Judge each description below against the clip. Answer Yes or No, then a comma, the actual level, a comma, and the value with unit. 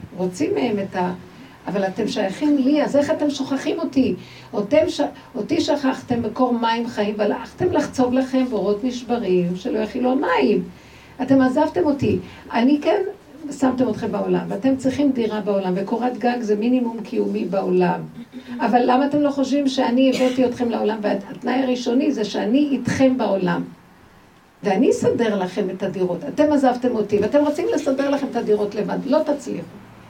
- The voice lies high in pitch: Yes, very high, 250 Hz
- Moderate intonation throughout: Yes, average, 4.8 semitones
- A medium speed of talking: No, fast, 155 wpm